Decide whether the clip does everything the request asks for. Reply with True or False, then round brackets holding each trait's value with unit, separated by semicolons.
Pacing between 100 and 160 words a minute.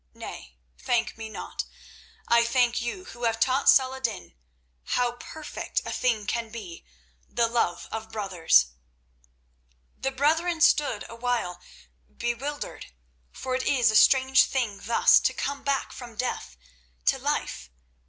True (140 wpm)